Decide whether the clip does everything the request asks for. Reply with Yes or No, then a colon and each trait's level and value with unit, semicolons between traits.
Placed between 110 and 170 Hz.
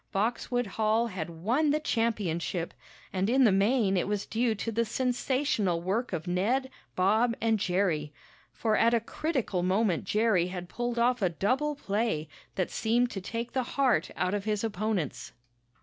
No: high, 215 Hz